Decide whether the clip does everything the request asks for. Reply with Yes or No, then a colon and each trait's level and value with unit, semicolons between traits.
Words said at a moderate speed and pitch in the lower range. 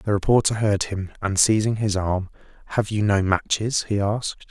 Yes: average, 185 wpm; low, 105 Hz